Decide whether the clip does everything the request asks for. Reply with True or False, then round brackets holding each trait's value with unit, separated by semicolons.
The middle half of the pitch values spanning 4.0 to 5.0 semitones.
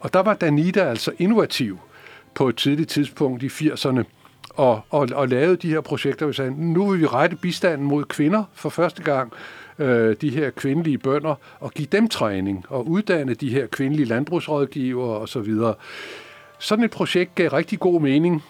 True (4.3 semitones)